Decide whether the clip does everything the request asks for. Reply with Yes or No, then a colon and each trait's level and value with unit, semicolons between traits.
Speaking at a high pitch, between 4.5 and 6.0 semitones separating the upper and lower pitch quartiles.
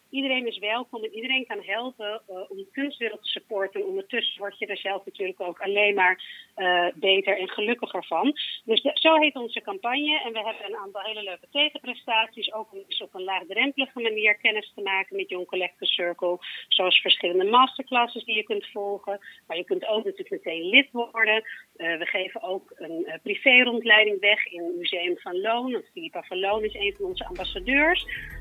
Yes: high, 215 Hz; average, 4.9 semitones